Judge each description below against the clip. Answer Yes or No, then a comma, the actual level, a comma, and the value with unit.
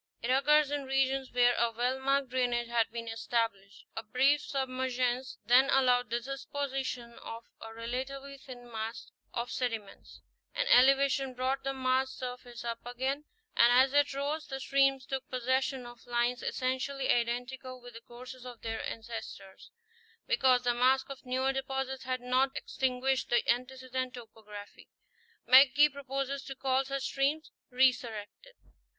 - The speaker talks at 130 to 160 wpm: Yes, average, 150 wpm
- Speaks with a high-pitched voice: Yes, very high, 255 Hz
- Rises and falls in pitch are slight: Yes, narrow, 2.0 semitones